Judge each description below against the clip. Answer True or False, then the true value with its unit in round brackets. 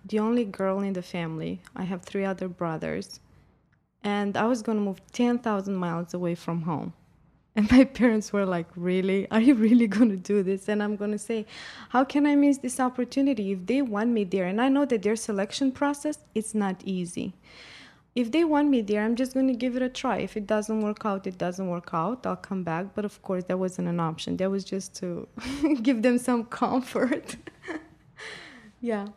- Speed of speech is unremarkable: False (210 wpm)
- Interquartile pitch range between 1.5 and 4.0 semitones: False (4.5 semitones)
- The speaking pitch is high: True (210 Hz)